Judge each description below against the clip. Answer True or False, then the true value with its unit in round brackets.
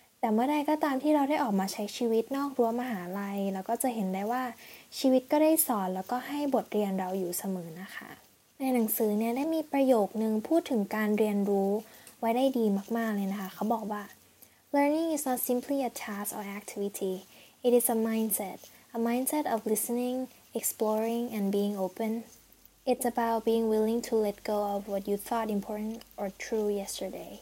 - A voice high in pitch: True (225 Hz)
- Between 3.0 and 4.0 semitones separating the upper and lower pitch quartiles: True (3.5 semitones)